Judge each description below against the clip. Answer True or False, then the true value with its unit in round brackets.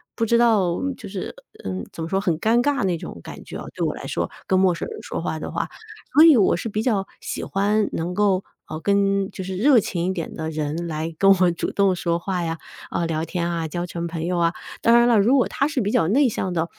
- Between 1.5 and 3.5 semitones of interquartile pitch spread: False (4.1 semitones)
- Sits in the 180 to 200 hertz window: True (190 Hz)